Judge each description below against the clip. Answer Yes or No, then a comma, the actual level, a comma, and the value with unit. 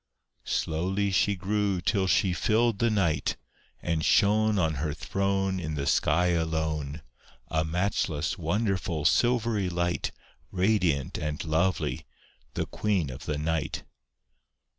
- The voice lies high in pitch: No, very low, 90 Hz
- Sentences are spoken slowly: Yes, slow, 120 wpm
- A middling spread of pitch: Yes, average, 4.0 semitones